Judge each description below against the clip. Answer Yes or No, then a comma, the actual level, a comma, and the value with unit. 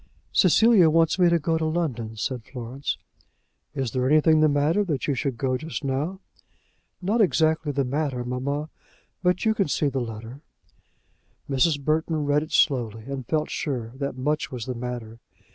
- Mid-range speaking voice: Yes, medium, 145 Hz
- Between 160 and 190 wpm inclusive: Yes, average, 170 wpm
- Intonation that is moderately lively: Yes, average, 4.0 semitones